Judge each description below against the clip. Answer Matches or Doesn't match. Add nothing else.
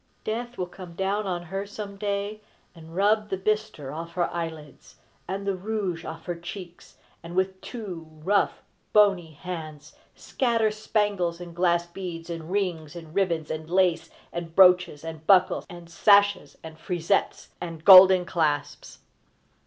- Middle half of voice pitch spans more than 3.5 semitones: Doesn't match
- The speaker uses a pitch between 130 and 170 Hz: Doesn't match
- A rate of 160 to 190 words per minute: Doesn't match